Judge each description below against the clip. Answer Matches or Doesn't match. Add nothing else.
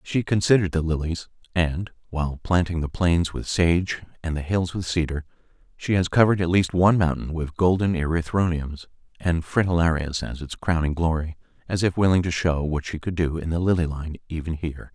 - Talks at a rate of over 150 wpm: Matches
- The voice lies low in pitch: Matches